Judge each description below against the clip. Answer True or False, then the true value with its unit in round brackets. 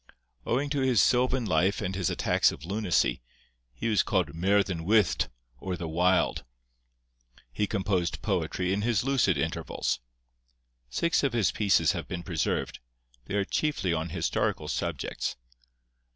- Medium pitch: False (95 Hz)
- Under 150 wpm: True (140 wpm)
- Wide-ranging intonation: False (4.6 semitones)